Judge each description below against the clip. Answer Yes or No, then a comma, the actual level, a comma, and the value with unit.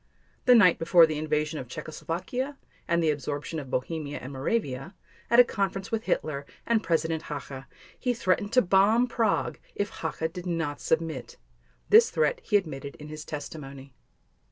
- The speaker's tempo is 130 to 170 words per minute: Yes, average, 160 wpm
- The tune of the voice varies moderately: No, wide, 5.7 semitones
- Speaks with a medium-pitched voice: Yes, medium, 165 Hz